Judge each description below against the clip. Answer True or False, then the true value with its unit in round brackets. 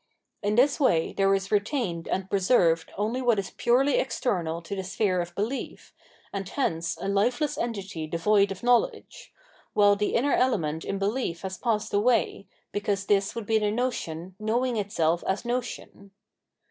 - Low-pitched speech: False (205 Hz)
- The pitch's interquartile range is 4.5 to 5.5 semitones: False (4.1 semitones)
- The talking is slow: False (160 wpm)